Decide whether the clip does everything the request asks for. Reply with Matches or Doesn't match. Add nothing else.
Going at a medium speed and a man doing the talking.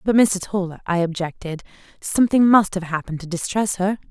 Doesn't match